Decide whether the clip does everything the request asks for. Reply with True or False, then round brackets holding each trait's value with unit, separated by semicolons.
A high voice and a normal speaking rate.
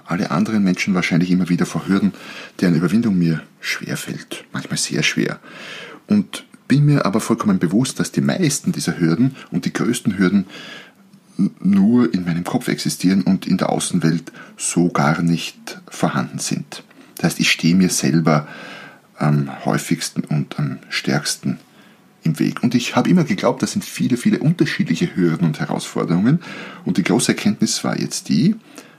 False (110 Hz; 160 wpm)